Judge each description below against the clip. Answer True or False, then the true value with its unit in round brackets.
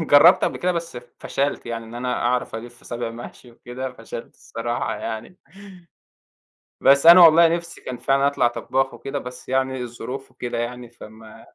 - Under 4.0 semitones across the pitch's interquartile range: True (2.9 semitones)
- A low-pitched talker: True (125 Hz)